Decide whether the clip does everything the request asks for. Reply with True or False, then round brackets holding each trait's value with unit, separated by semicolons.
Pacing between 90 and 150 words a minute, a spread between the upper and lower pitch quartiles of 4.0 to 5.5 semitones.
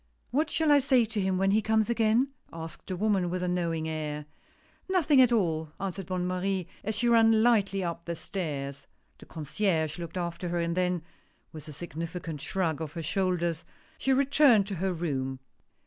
False (190 wpm; 4.8 semitones)